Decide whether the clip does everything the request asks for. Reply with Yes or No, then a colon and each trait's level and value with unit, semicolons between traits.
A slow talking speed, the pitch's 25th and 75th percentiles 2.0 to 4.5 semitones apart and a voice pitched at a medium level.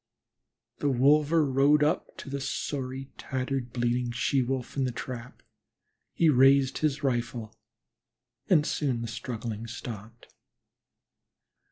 No: slow, 120 wpm; average, 2.8 semitones; low, 130 Hz